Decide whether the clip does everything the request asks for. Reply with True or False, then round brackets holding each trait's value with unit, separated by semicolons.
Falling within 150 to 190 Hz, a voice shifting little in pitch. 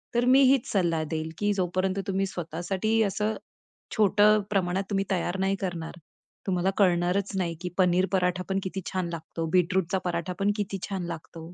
True (185 Hz; 2.2 semitones)